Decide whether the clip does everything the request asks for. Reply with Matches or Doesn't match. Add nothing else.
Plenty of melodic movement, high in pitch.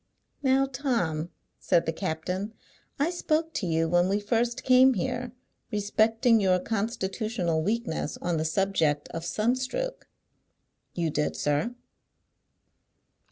Matches